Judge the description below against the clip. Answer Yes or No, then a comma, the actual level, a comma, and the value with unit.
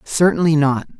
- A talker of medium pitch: Yes, medium, 155 Hz